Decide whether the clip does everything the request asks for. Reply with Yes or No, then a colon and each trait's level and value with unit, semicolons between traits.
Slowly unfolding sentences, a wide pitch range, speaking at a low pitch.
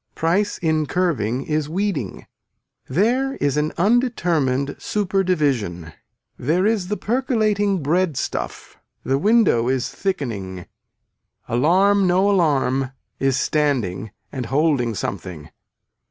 No: slow, 110 wpm; wide, 7.2 semitones; medium, 155 Hz